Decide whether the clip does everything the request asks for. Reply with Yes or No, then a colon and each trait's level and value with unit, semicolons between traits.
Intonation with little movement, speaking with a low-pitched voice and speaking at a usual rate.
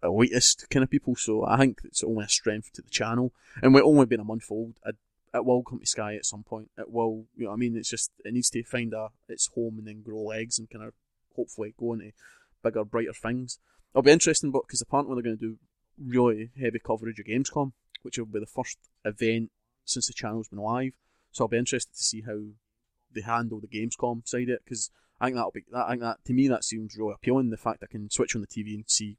No: narrow, 2.2 semitones; low, 115 Hz; fast, 245 wpm